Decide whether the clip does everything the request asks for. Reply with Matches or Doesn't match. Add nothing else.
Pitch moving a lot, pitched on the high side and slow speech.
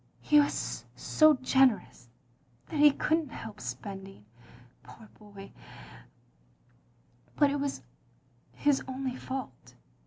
Matches